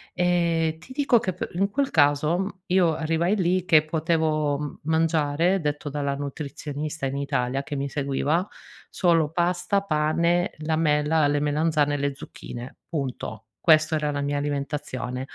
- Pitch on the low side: No, medium, 155 Hz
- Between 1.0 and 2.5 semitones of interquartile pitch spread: No, average, 2.9 semitones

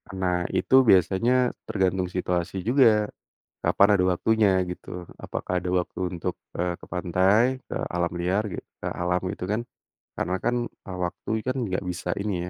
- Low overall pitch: Yes, very low, 95 Hz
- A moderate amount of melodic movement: Yes, average, 3.0 semitones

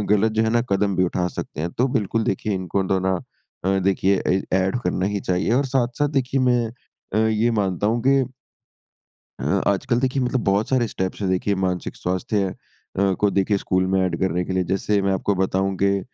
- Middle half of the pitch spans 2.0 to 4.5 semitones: Yes, average, 3.3 semitones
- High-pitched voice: No, low, 100 Hz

